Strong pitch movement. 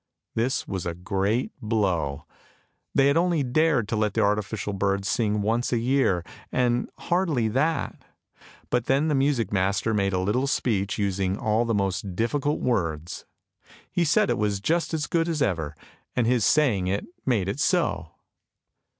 Yes: wide, 5.8 semitones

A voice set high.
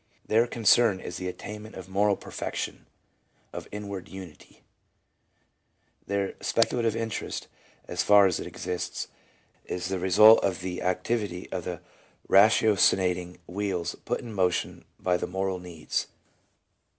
No: very low, 95 Hz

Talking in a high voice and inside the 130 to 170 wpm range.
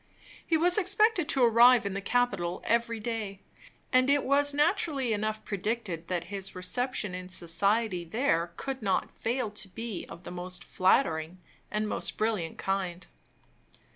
Yes: high, 215 Hz; average, 150 wpm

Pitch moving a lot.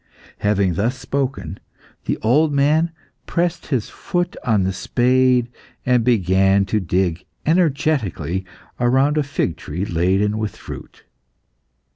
Yes: wide, 6.5 semitones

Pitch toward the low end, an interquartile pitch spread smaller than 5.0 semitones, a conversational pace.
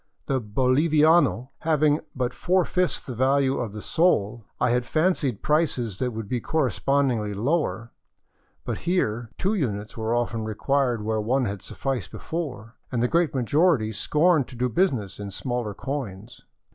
No: low, 125 Hz; average, 5.3 semitones; average, 150 wpm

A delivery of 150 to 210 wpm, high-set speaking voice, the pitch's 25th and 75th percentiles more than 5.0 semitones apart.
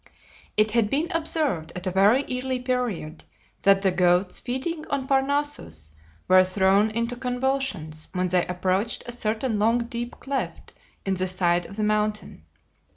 Yes: average, 155 wpm; high, 215 Hz; wide, 5.6 semitones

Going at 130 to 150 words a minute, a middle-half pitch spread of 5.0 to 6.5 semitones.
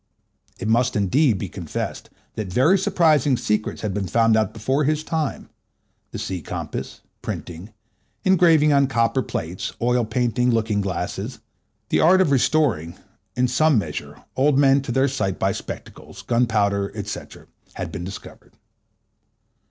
Yes: average, 140 wpm; wide, 5.4 semitones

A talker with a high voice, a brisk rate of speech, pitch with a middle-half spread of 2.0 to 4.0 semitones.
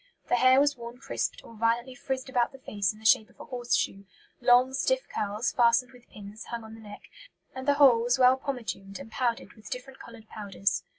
Yes: high, 240 Hz; fast, 220 wpm; average, 3.0 semitones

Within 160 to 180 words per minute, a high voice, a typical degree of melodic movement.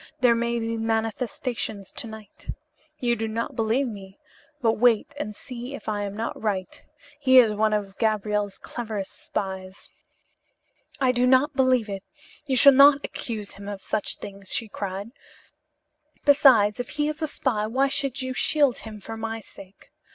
Yes: average, 165 wpm; high, 225 Hz; average, 3.7 semitones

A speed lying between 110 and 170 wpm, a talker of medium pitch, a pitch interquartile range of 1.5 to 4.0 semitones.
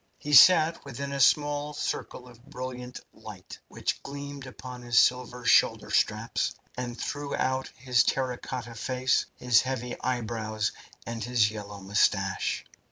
No: average, 140 wpm; low, 125 Hz; narrow, 2.5 semitones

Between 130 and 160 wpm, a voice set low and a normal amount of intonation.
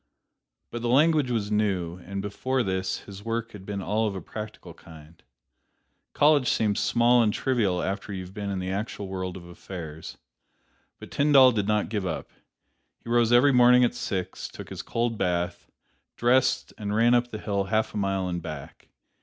No: average, 185 wpm; low, 105 Hz; average, 4.1 semitones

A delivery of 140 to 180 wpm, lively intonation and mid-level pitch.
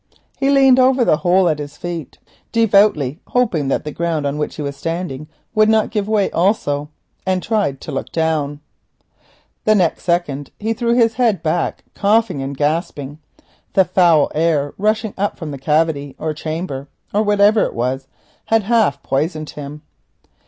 Yes: average, 165 wpm; wide, 6.3 semitones; medium, 170 Hz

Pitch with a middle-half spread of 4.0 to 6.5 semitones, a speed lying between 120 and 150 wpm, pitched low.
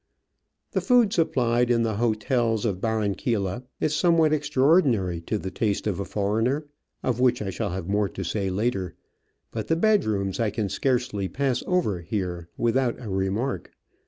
No: average, 4.9 semitones; average, 170 wpm; low, 110 Hz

